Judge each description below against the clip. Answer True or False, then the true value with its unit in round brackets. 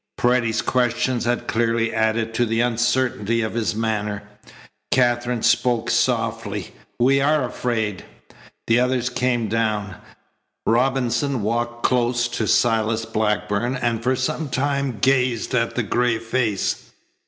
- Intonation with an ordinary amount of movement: False (1.9 semitones)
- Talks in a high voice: False (120 Hz)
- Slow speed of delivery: True (125 wpm)